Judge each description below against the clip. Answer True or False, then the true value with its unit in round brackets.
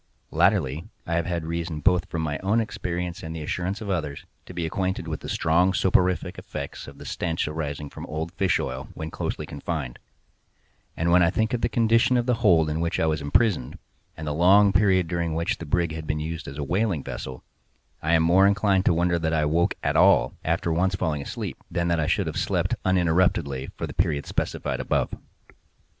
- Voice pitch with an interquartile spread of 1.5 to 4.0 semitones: True (3.0 semitones)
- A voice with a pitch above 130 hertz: False (85 Hz)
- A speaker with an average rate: False (210 wpm)